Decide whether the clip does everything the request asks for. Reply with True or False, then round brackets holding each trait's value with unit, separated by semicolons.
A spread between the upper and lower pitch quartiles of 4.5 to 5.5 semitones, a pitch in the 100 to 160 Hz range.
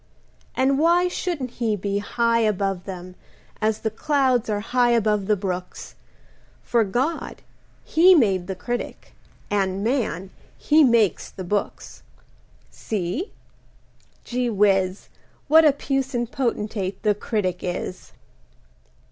False (4.9 semitones; 220 Hz)